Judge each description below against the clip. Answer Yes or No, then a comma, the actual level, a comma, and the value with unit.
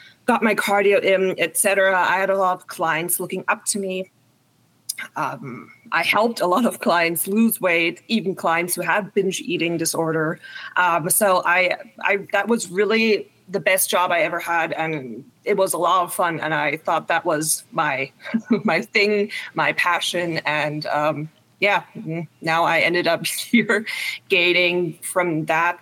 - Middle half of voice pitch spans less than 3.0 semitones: No, average, 3.5 semitones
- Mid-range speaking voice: Yes, medium, 180 Hz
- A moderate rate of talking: Yes, average, 170 wpm